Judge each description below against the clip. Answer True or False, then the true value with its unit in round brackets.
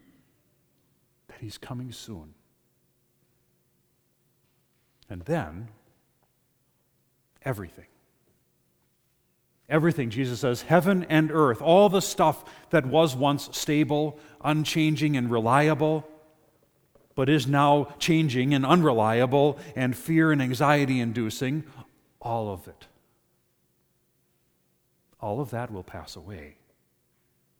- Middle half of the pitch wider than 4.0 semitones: True (4.6 semitones)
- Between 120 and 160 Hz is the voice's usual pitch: True (140 Hz)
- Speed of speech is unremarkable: False (90 wpm)